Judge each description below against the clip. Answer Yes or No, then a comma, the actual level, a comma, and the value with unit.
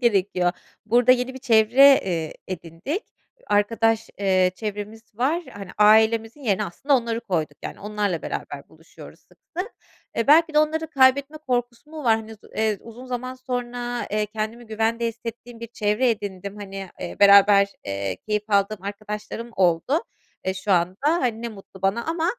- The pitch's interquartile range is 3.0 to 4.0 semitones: Yes, average, 3.7 semitones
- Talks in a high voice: Yes, high, 220 Hz